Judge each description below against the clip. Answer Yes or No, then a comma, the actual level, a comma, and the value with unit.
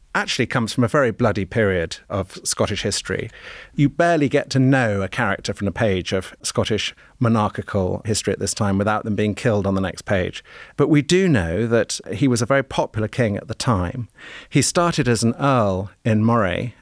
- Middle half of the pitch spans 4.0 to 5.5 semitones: Yes, average, 4.6 semitones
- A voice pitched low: Yes, low, 115 Hz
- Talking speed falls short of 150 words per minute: No, average, 200 wpm